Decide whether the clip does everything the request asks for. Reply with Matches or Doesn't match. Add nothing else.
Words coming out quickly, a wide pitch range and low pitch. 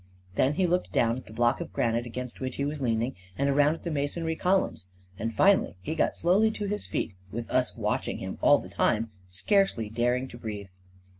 Matches